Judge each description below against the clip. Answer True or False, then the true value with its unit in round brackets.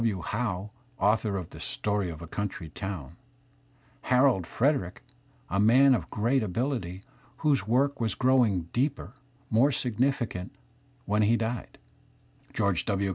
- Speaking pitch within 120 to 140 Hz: False (105 Hz)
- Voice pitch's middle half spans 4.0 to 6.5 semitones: True (4.9 semitones)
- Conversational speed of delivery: False (130 wpm)